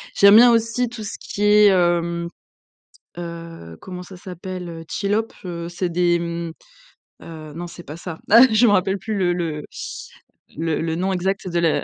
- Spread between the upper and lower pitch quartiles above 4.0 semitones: No, average, 2.8 semitones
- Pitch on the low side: No, medium, 175 Hz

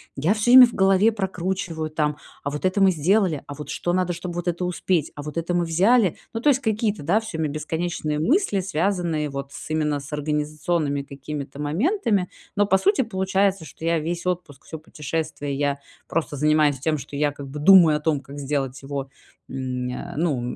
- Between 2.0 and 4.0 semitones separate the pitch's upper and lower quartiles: No, average, 4.5 semitones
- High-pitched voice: No, medium, 160 Hz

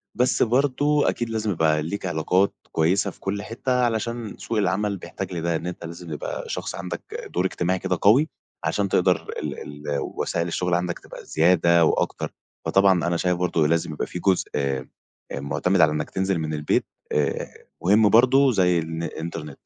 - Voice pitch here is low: Yes, very low, 90 Hz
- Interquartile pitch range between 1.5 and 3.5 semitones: No, average, 4.0 semitones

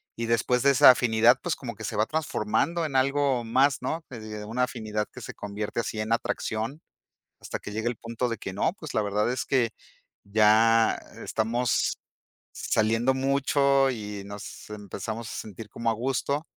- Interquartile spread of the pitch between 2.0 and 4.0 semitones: Yes, average, 3.5 semitones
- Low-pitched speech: Yes, low, 115 Hz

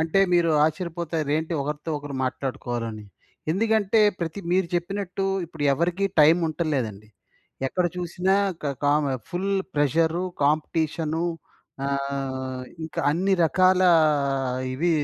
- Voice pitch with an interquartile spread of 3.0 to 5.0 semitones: Yes, average, 3.7 semitones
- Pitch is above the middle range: No, medium, 160 Hz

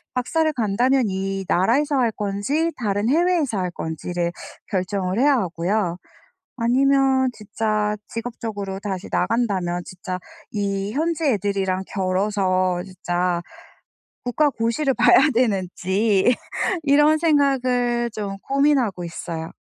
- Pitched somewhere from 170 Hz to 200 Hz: No, high, 210 Hz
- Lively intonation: Yes, wide, 5.7 semitones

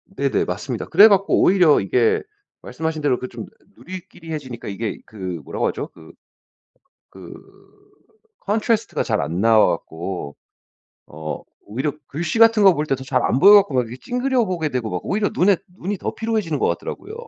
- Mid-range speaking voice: Yes, medium, 145 Hz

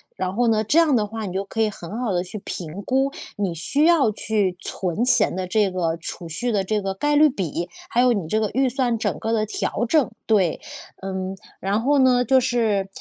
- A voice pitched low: No, high, 215 Hz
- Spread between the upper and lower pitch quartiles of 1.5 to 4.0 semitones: No, average, 4.7 semitones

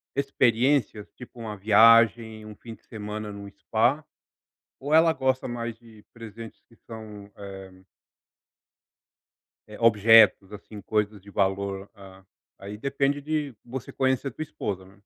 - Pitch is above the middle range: No, low, 110 Hz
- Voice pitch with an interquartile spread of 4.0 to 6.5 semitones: No, average, 3.3 semitones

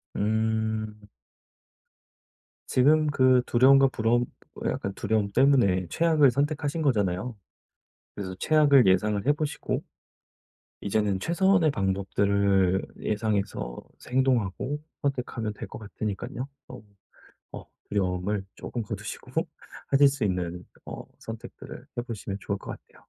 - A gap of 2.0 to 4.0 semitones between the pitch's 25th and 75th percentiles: No, wide, 5.4 semitones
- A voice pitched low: Yes, low, 110 Hz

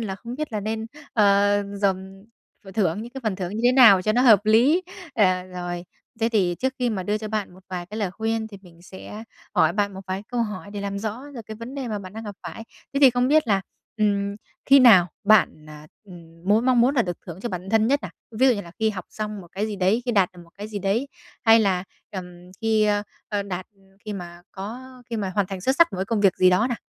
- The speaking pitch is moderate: No, high, 205 Hz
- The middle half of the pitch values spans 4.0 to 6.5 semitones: No, average, 3.2 semitones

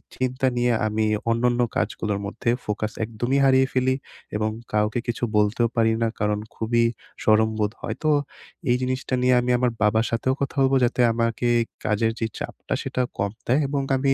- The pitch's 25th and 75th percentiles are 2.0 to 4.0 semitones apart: Yes, average, 2.8 semitones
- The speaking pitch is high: No, low, 115 Hz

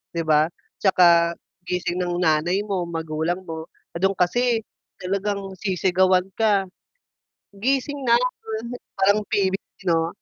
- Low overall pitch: No, medium, 185 Hz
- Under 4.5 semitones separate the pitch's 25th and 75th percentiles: Yes, average, 2.9 semitones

